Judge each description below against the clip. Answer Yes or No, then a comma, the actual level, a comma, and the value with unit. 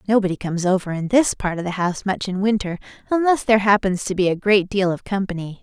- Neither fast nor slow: No, fast, 235 wpm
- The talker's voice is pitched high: Yes, high, 195 Hz